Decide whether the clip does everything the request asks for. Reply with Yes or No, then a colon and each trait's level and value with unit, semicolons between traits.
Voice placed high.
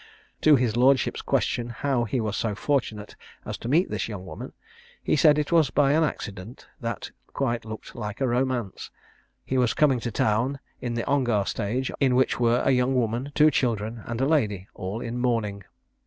No: low, 120 Hz